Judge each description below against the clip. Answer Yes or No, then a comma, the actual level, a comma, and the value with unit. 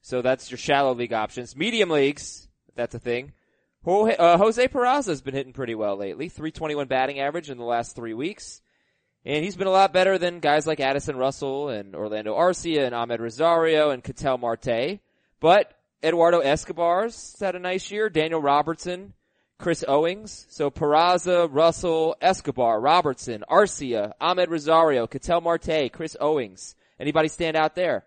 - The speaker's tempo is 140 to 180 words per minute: Yes, average, 160 wpm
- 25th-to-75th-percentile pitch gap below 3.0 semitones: No, average, 4.6 semitones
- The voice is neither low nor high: Yes, medium, 155 Hz